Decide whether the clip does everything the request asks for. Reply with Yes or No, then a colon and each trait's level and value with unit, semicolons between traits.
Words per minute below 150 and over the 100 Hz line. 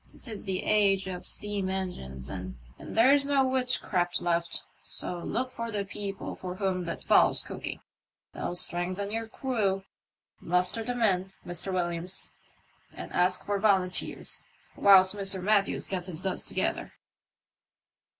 Yes: average, 140 wpm; high, 190 Hz